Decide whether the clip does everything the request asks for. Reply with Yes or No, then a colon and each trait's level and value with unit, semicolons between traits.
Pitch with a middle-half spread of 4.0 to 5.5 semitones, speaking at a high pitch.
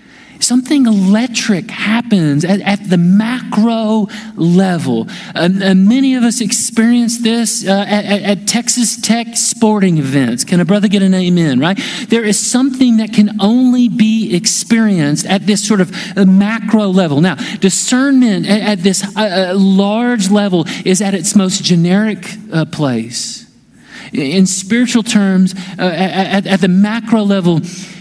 No: average, 3.2 semitones; high, 205 Hz